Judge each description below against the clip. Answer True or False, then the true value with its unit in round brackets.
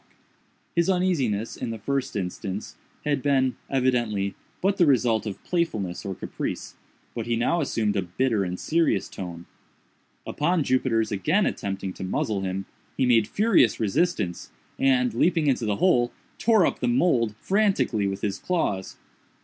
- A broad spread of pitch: True (6.9 semitones)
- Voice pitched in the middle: False (120 Hz)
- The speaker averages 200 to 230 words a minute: False (150 wpm)